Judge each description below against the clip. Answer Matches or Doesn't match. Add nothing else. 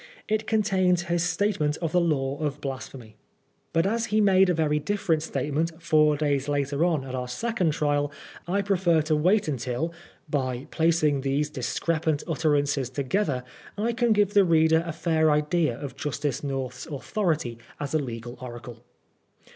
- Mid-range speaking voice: Matches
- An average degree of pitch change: Matches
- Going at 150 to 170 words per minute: Matches